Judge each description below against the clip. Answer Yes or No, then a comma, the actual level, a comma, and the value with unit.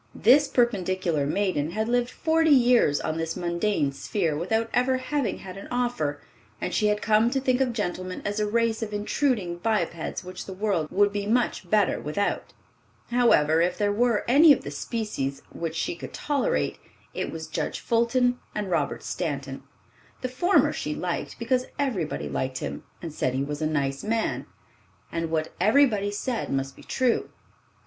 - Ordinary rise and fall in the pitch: No, wide, 6.6 semitones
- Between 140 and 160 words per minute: No, average, 170 wpm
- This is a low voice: No, high, 205 Hz